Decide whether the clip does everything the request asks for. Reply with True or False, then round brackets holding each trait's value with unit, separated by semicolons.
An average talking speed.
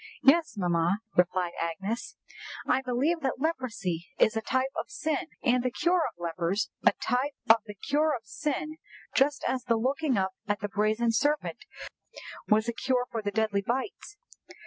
True (170 wpm)